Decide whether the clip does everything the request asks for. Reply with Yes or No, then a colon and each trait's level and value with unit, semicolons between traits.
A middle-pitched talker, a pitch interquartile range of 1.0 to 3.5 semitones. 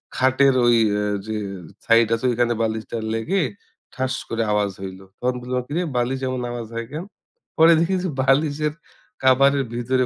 No: low, 125 Hz; average, 3.1 semitones